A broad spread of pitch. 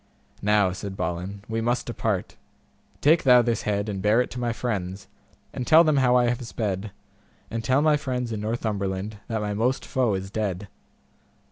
No: average, 3.7 semitones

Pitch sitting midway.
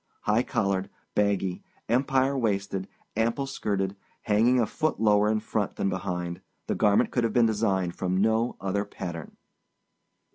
No: low, 105 Hz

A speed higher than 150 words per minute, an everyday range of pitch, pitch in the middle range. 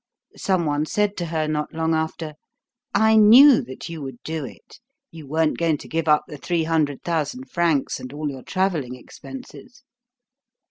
Yes: average, 175 wpm; average, 3.7 semitones; medium, 160 Hz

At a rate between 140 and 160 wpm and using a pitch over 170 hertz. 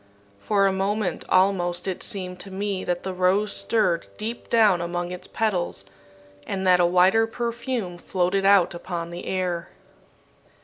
Yes: average, 150 wpm; medium, 185 Hz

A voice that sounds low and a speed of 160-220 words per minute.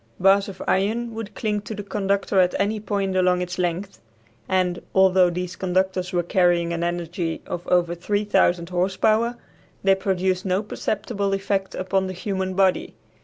No: high, 190 Hz; average, 165 wpm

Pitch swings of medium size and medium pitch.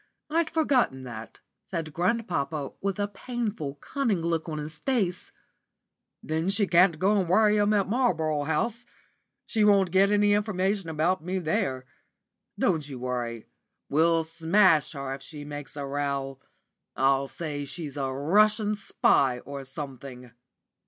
No: wide, 6.5 semitones; medium, 165 Hz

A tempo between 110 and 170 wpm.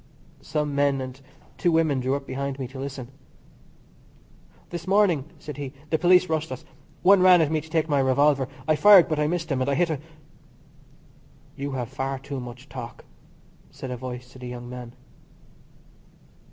No: average, 180 wpm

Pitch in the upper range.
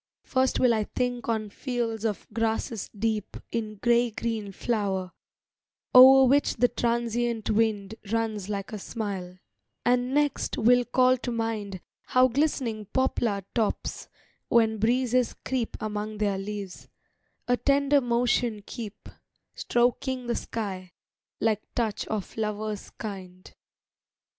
Yes: high, 225 Hz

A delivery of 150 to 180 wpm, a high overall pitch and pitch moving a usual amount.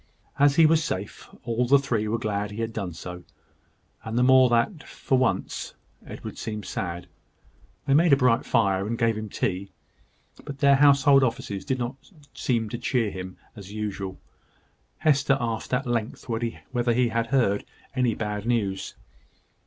No: average, 165 wpm; low, 115 Hz; average, 3.9 semitones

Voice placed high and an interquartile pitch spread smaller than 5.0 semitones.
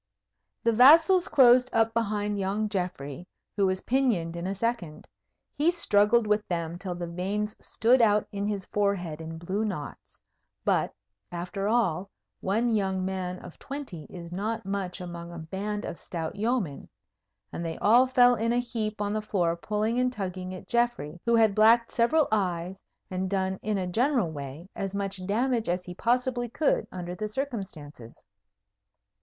Yes: high, 200 Hz; average, 4.4 semitones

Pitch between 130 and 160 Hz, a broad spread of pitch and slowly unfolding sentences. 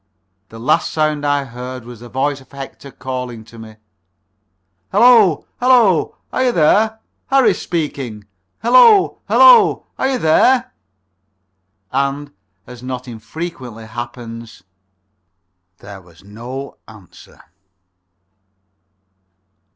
Yes: low, 135 Hz; wide, 7.5 semitones; slow, 105 wpm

